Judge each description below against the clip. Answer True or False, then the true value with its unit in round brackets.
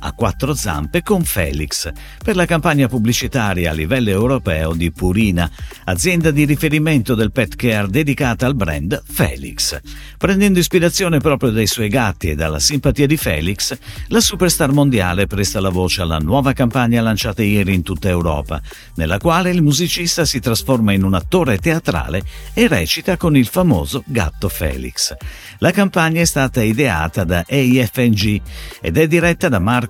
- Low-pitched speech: True (120 Hz)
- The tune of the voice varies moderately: False (8.5 semitones)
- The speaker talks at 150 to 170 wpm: True (155 wpm)